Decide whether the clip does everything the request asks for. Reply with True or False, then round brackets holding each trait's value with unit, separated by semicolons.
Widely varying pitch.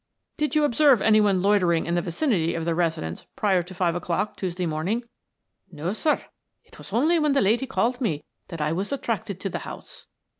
True (5.9 semitones)